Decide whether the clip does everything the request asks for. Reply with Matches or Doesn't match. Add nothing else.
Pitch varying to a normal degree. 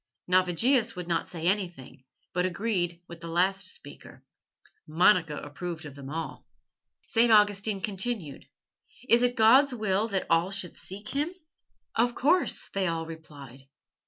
Matches